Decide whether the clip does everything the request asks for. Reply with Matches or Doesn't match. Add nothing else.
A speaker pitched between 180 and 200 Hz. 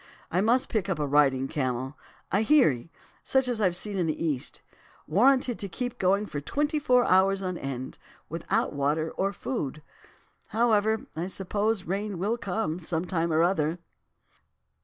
Matches